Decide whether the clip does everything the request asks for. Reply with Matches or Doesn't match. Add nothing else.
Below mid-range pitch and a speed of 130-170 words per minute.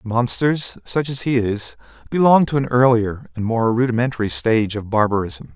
Matches